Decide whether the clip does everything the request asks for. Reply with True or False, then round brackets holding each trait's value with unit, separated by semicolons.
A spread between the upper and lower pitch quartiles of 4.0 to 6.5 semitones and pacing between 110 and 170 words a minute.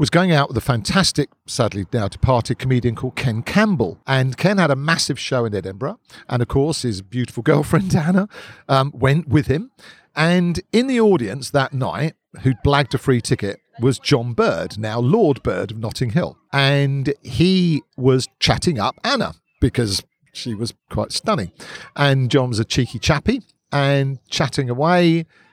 True (4.4 semitones; 165 wpm)